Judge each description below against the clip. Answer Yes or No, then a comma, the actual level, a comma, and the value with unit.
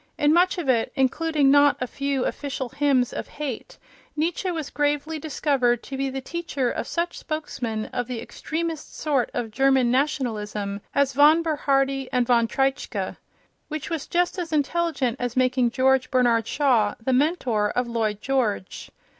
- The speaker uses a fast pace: No, average, 155 wpm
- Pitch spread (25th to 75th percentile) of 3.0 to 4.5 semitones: Yes, average, 3.6 semitones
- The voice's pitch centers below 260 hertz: No, very high, 270 Hz